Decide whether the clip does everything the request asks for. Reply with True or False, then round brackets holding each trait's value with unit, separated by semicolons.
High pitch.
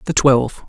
False (135 Hz)